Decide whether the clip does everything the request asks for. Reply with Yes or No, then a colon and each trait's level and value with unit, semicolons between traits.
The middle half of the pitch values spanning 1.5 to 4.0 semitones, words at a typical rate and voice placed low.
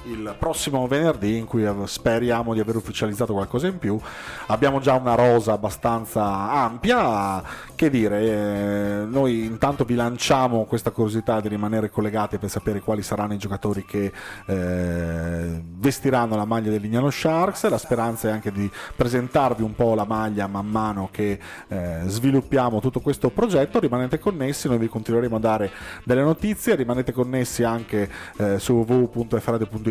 Yes: average, 3.3 semitones; average, 155 wpm; low, 115 Hz